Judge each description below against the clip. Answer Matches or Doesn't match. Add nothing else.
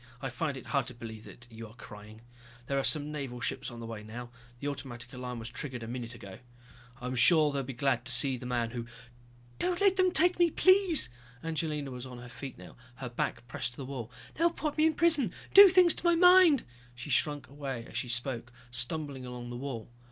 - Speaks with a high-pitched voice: Doesn't match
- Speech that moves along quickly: Matches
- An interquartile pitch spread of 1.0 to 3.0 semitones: Doesn't match